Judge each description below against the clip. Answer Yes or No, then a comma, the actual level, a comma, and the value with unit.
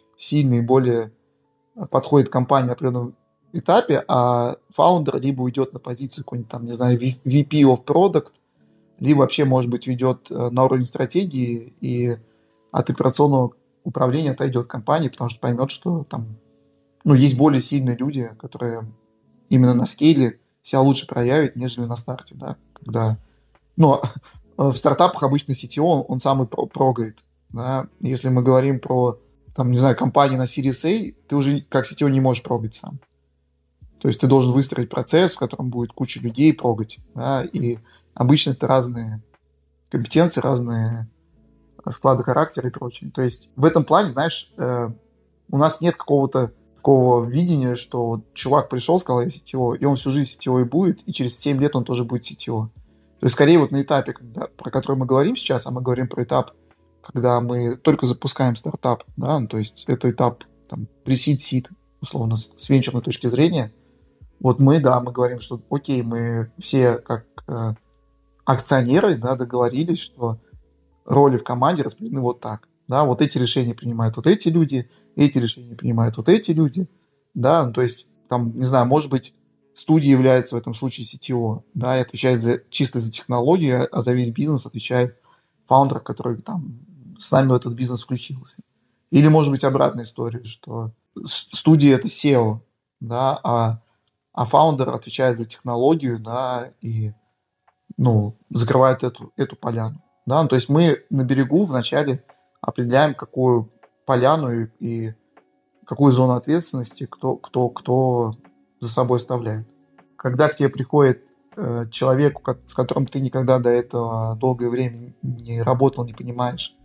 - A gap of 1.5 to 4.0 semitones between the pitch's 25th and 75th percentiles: Yes, average, 2.7 semitones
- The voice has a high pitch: No, low, 125 Hz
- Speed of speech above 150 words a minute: Yes, fast, 160 wpm